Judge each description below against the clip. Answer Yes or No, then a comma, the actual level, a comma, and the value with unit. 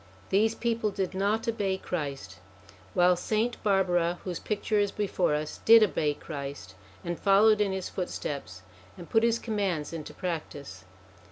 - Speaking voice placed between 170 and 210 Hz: Yes, high, 190 Hz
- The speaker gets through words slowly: No, average, 150 wpm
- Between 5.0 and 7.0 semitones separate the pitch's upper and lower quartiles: Yes, wide, 5.5 semitones